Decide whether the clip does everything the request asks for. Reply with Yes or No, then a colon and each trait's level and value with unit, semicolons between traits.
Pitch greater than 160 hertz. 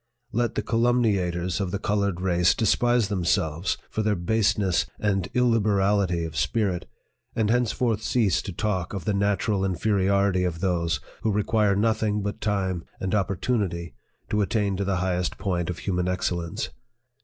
No: low, 100 Hz